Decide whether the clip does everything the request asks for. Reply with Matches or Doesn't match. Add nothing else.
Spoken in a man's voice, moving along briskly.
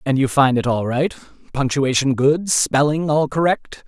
Doesn't match